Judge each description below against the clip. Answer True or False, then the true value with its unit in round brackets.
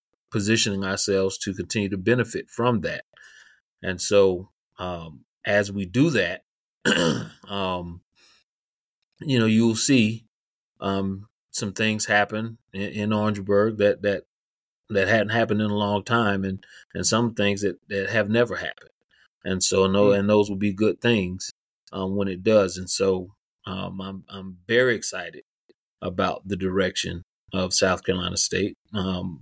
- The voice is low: True (100 Hz)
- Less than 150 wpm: False (155 wpm)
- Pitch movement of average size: False (2.3 semitones)